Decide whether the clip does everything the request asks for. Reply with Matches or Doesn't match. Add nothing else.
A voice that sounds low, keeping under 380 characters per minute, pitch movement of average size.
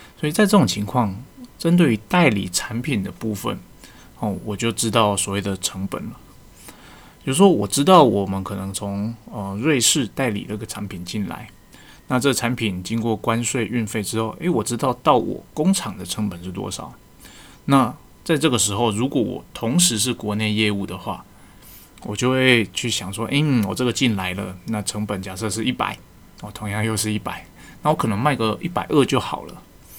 Matches